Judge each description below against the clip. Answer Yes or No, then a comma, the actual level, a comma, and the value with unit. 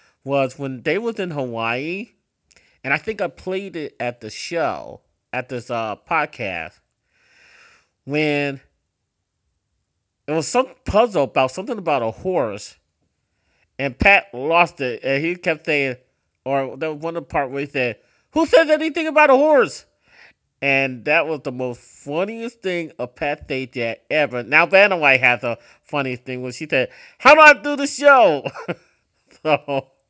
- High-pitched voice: No, medium, 140 Hz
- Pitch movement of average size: No, wide, 6.6 semitones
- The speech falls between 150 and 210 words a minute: Yes, average, 165 wpm